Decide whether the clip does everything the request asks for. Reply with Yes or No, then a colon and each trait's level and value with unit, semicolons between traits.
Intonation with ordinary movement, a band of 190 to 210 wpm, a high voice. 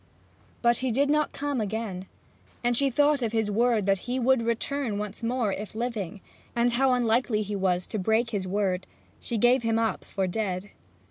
Yes: average, 3.3 semitones; average, 195 wpm; high, 225 Hz